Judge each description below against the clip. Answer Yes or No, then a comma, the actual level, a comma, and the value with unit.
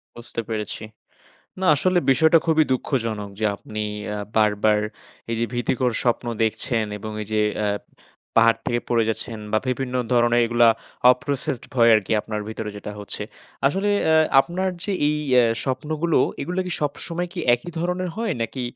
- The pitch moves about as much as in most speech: No, wide, 6.2 semitones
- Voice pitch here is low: Yes, low, 120 Hz